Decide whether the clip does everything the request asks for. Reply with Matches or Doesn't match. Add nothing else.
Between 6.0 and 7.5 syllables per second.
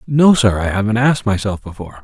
Matches